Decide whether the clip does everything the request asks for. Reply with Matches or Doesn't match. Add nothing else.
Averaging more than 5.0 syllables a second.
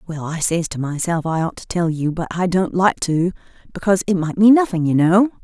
Matches